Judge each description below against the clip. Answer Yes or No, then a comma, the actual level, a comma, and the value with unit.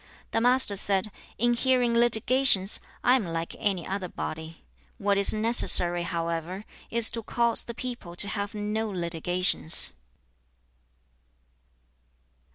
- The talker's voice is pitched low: No, high, 205 Hz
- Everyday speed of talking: No, slow, 120 wpm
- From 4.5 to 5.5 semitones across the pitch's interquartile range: Yes, average, 5.0 semitones